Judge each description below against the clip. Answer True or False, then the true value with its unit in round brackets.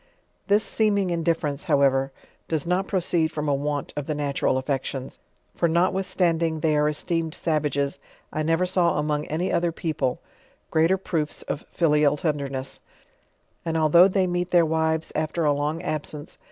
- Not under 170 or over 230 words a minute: False (155 wpm)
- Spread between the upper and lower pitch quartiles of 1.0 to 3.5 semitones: True (2.6 semitones)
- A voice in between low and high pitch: True (160 Hz)